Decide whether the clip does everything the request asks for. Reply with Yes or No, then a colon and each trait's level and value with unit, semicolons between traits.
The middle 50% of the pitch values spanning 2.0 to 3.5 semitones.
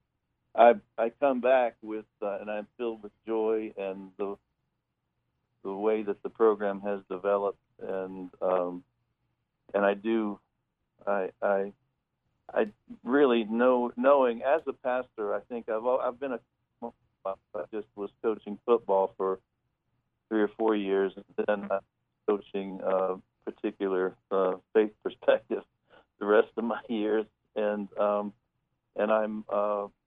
Yes: average, 2.7 semitones